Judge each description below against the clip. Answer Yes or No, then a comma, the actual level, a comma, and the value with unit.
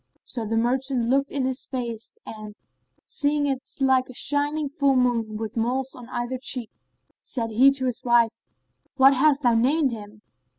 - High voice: Yes, very high, 255 Hz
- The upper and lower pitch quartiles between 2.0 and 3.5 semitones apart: Yes, average, 2.9 semitones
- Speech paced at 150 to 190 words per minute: Yes, average, 170 wpm